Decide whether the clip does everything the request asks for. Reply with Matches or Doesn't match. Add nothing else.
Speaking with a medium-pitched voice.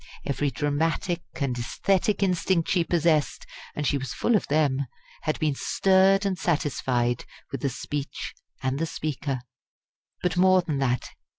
Matches